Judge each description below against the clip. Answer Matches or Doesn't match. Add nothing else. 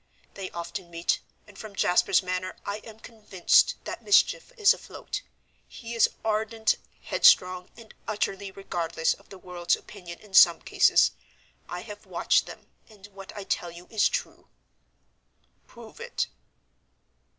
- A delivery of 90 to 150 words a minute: Matches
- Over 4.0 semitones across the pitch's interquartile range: Doesn't match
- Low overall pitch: Doesn't match